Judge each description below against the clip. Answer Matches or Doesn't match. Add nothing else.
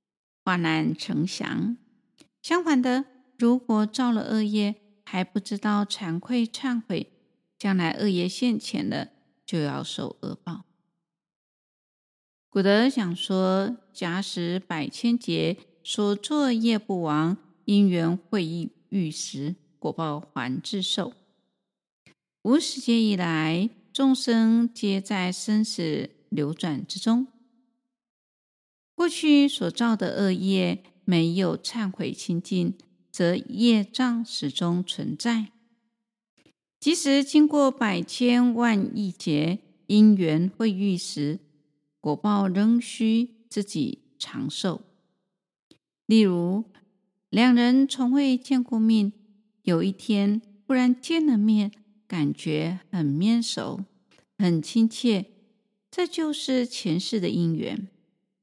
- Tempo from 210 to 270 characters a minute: Doesn't match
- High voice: Matches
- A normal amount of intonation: Matches